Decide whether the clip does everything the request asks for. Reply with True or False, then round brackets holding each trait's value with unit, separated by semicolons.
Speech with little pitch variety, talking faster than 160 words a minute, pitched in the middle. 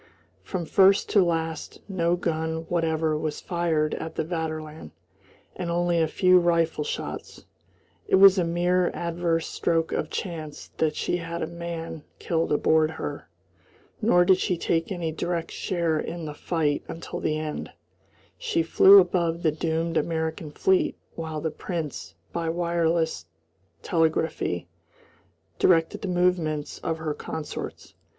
False (1.5 semitones; 140 wpm; 165 Hz)